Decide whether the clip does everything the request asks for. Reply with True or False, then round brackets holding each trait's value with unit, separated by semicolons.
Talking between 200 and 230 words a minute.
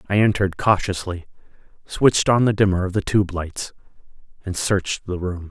False (165 wpm)